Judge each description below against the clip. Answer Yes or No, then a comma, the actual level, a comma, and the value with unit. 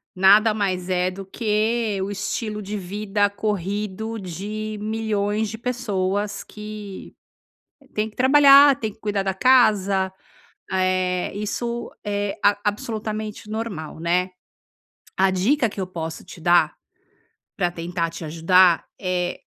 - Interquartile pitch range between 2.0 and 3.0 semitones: Yes, average, 2.7 semitones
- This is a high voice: Yes, high, 205 Hz